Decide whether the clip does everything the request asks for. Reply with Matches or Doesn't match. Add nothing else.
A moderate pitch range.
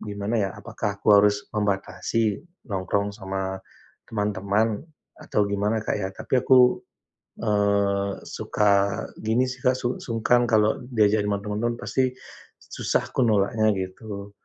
Doesn't match